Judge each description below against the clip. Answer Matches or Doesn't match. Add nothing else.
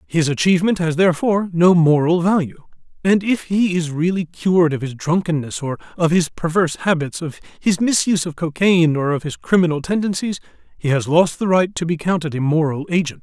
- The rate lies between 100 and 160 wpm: Doesn't match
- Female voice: Doesn't match